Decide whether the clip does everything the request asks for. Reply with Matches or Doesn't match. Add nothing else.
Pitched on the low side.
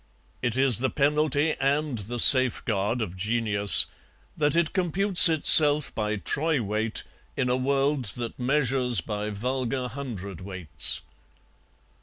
Matches